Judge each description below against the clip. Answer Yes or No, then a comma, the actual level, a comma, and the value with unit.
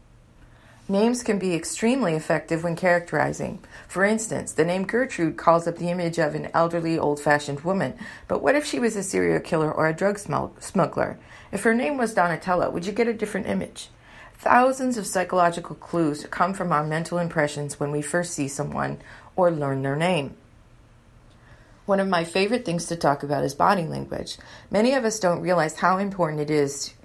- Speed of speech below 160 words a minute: No, average, 185 wpm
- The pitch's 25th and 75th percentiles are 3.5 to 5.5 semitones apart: Yes, average, 4.8 semitones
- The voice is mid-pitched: Yes, medium, 170 Hz